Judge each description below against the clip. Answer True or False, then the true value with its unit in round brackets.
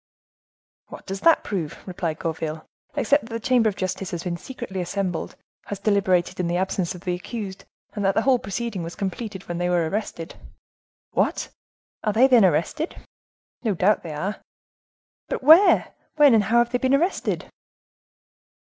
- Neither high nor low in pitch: False (195 Hz)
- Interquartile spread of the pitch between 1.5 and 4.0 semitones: False (4.9 semitones)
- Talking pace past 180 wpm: False (170 wpm)